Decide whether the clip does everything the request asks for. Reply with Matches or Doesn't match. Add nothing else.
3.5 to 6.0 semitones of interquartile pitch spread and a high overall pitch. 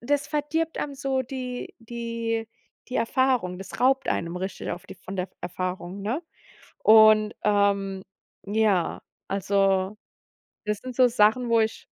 Matches